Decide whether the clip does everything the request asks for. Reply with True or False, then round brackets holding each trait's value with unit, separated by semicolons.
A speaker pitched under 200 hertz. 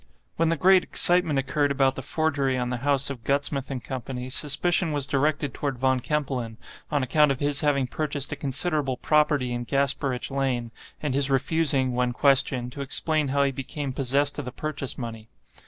True (140 Hz)